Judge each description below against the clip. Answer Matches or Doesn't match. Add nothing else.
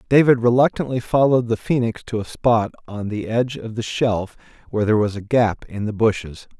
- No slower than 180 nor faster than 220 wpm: Matches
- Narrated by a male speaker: Matches